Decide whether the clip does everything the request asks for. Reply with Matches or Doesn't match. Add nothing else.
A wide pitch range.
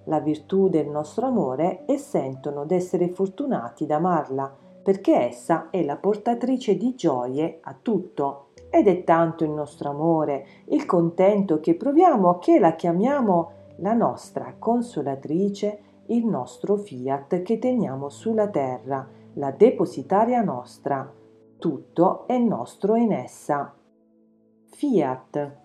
Matches